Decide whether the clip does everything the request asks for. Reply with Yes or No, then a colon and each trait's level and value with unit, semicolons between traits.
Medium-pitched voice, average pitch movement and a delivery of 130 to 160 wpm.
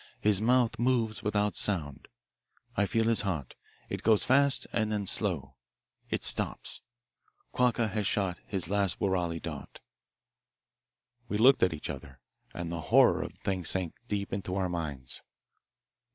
No: low, 100 Hz; average, 4.1 semitones; average, 150 wpm